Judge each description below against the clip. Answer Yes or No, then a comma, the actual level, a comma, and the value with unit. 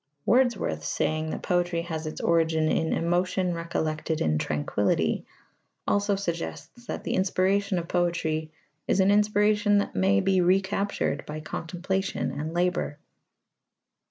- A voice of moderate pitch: Yes, medium, 175 Hz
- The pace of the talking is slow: Yes, slow, 130 wpm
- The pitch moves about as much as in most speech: Yes, average, 3.8 semitones